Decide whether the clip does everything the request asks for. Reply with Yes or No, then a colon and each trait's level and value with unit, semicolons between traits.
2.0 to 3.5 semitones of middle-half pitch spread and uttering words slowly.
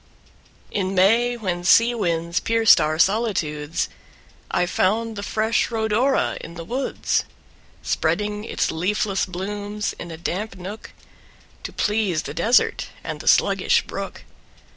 No: average, 4.1 semitones; slow, 130 wpm